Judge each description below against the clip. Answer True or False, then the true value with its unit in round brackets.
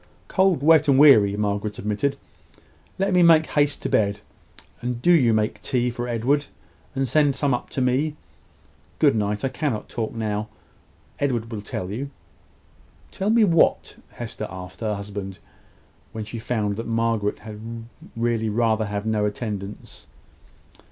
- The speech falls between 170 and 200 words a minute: False (150 wpm)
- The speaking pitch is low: True (115 Hz)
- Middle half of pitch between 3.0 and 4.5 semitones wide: False (4.9 semitones)